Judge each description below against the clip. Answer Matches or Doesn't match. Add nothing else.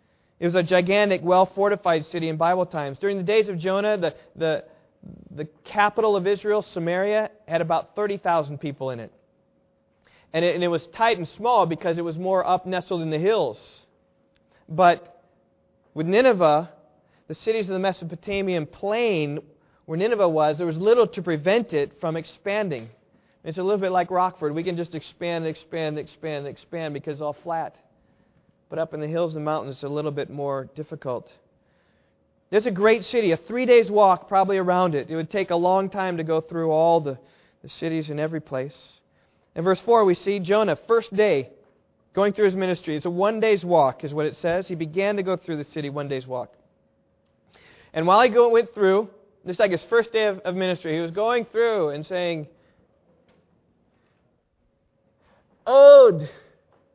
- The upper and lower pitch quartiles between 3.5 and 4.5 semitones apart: Matches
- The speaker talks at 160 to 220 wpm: Matches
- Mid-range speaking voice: Matches